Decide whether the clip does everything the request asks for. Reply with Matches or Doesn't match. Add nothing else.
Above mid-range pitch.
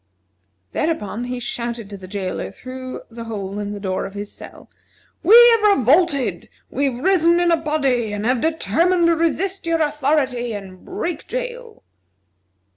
Matches